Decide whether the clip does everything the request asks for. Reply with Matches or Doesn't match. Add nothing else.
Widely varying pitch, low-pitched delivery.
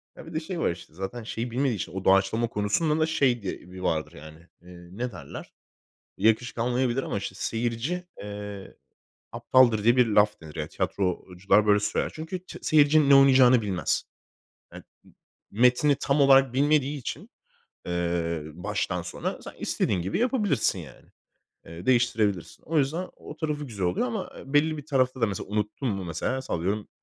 Matches